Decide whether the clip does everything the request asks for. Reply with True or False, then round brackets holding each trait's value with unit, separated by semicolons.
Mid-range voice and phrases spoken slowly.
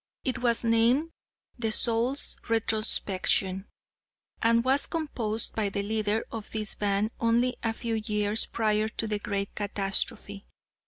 False (220 Hz; 130 wpm)